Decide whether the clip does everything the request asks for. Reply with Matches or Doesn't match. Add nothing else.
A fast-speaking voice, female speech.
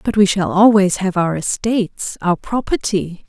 Doesn't match